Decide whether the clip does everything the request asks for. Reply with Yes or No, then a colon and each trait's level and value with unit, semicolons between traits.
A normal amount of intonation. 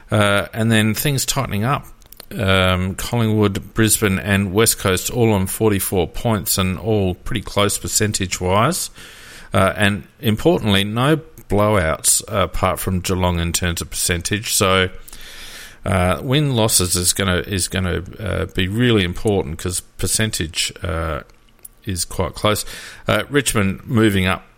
Yes: average, 3.0 semitones